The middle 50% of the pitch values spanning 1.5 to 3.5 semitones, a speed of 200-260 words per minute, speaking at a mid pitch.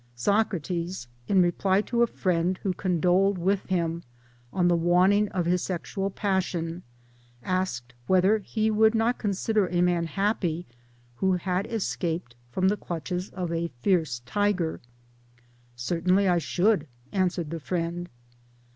No: narrow, 2.6 semitones; average, 140 wpm; medium, 180 Hz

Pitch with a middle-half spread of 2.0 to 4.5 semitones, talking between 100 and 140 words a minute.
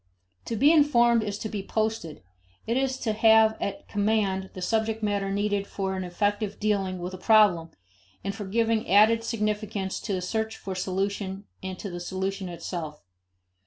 No: narrow, 2.6 semitones; average, 170 wpm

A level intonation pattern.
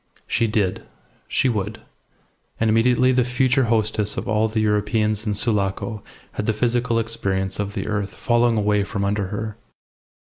Yes: narrow, 2.1 semitones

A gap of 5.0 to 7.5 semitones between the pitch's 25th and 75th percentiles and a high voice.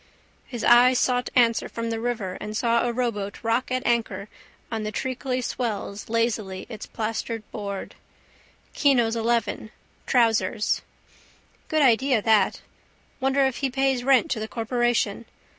No: narrow, 2.5 semitones; high, 235 Hz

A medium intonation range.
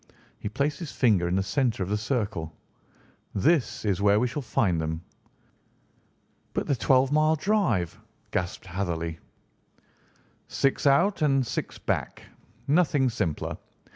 No: wide, 7.5 semitones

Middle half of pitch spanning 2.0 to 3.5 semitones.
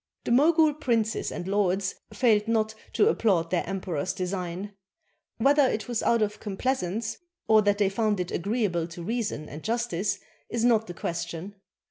No: average, 4.2 semitones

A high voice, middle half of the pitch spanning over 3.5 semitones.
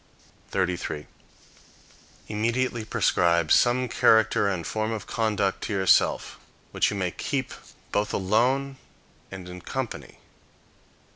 No: low, 105 Hz; average, 4.1 semitones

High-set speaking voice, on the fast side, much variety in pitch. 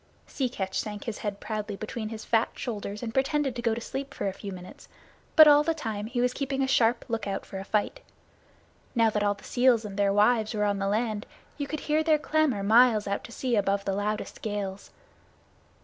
No: high, 220 Hz; fast, 220 wpm; average, 3.7 semitones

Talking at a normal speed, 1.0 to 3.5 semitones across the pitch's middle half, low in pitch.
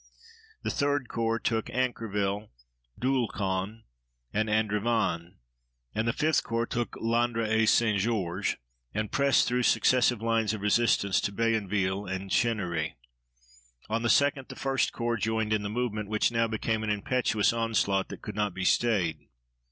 Yes: average, 150 wpm; narrow, 2.6 semitones; low, 110 Hz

